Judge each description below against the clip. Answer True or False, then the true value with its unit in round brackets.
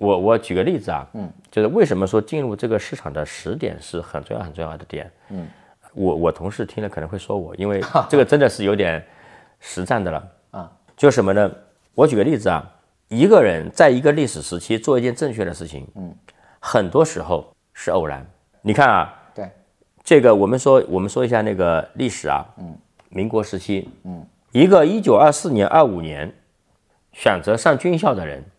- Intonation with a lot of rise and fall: False (4.3 semitones)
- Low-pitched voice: True (100 Hz)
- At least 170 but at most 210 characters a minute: False (275 characters per minute)